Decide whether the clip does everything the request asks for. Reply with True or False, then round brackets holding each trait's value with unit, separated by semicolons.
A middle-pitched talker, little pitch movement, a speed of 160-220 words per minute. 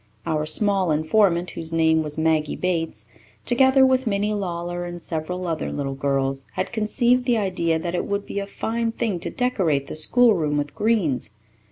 False (175 Hz; 5.2 semitones; 175 wpm)